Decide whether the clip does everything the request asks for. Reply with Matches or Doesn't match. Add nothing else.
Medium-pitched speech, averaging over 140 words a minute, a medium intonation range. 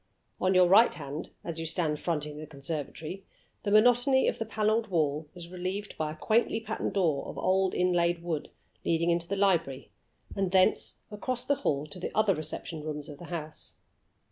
Matches